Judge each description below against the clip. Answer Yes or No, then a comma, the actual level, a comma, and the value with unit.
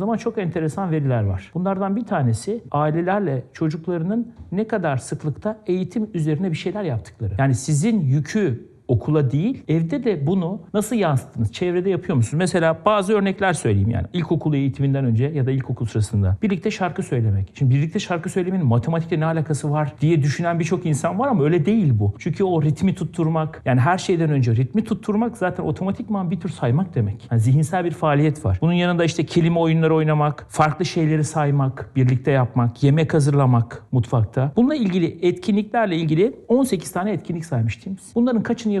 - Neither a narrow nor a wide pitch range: No, wide, 5.7 semitones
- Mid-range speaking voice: Yes, medium, 160 Hz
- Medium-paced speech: No, fast, 165 wpm